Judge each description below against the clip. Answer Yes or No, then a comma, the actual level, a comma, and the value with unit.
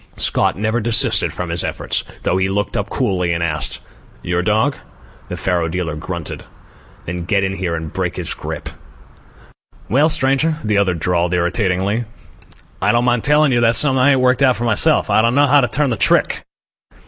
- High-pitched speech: No, low, 105 Hz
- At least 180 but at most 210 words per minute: Yes, average, 190 wpm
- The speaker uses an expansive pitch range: Yes, wide, 6.1 semitones